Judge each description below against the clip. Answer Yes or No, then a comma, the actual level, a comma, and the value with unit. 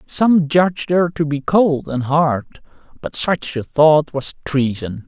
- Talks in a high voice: No, medium, 150 Hz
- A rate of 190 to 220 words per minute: No, average, 165 wpm